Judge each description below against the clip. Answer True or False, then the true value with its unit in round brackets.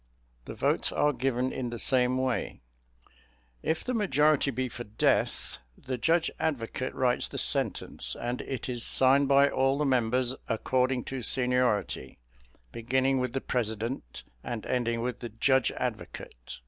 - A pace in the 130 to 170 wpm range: True (145 wpm)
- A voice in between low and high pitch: False (130 Hz)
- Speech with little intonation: True (1.9 semitones)